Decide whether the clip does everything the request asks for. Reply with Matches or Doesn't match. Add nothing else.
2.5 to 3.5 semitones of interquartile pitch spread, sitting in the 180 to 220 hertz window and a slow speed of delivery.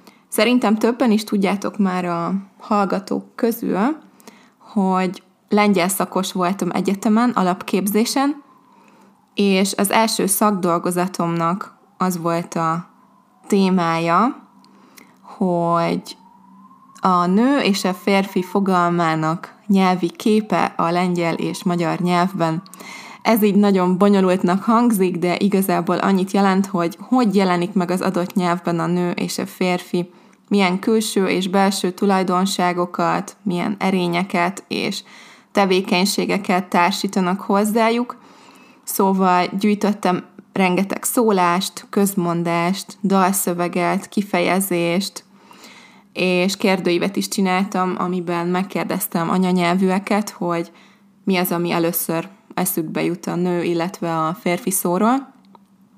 Matches